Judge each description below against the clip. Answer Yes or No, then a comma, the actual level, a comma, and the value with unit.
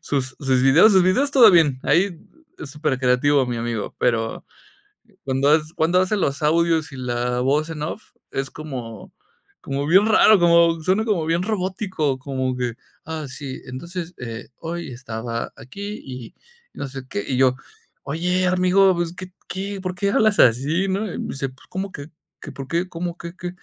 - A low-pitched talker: No, medium, 155 Hz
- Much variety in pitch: Yes, wide, 5.8 semitones